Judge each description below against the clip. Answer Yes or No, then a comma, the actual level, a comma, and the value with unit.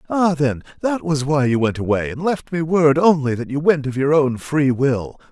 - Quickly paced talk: Yes, fast, 235 wpm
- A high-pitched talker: No, medium, 145 Hz